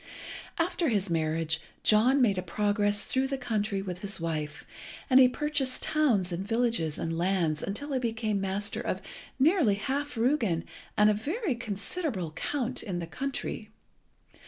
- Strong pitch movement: Yes, wide, 6.2 semitones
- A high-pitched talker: Yes, high, 210 Hz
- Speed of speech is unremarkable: Yes, average, 155 wpm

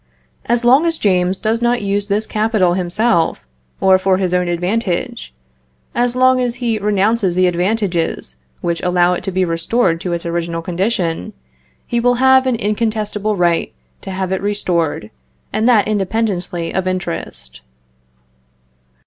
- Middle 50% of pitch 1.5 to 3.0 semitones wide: No, average, 4.3 semitones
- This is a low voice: No, high, 195 Hz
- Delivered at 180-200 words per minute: No, average, 150 wpm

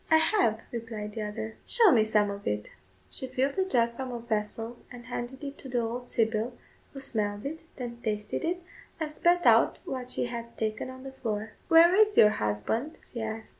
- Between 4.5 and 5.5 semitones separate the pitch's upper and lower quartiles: No, average, 3.8 semitones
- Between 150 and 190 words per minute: No, fast, 205 wpm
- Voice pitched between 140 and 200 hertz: No, high, 235 Hz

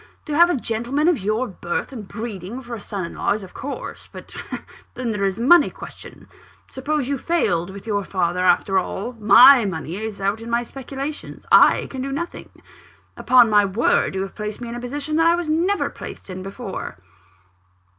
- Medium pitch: No, high, 230 Hz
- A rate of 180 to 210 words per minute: Yes, average, 200 wpm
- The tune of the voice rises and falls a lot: Yes, wide, 5.7 semitones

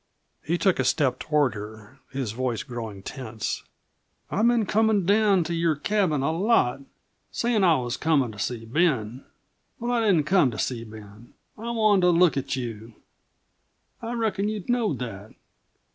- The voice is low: No, medium, 150 Hz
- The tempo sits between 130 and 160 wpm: No, average, 170 wpm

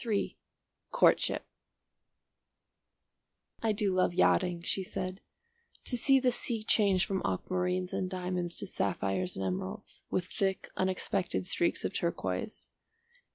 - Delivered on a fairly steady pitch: Yes, narrow, 2.2 semitones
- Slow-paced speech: Yes, slow, 120 wpm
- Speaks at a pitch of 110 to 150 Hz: No, medium, 185 Hz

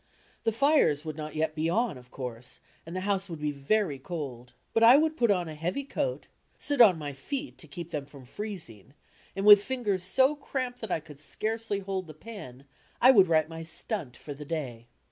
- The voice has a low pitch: No, medium, 170 Hz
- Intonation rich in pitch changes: Yes, wide, 7.0 semitones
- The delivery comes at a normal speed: No, fast, 210 wpm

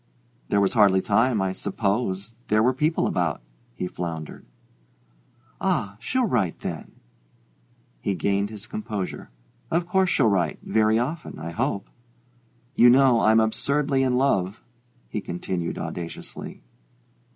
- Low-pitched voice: Yes, low, 105 Hz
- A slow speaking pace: Yes, slow, 130 wpm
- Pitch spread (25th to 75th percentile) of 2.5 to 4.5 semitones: No, average, 5.0 semitones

